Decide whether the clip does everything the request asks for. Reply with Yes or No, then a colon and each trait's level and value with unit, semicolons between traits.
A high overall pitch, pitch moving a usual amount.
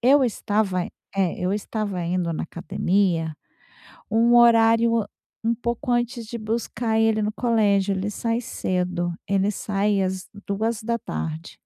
Yes: high, 210 Hz; average, 3.6 semitones